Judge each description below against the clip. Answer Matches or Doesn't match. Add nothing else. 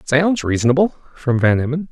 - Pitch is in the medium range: Matches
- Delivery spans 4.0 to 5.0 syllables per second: Doesn't match